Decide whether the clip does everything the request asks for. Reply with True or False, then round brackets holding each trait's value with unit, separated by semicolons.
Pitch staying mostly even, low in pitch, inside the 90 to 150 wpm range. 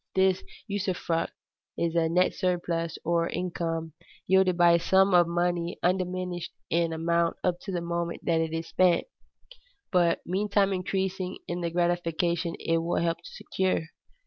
False (1.5 semitones; 175 Hz; 145 wpm)